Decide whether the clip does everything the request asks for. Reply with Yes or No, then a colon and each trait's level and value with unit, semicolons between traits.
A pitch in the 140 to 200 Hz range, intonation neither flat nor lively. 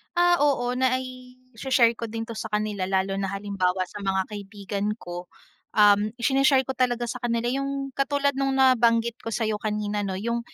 No: high, 230 Hz; average, 3.9 semitones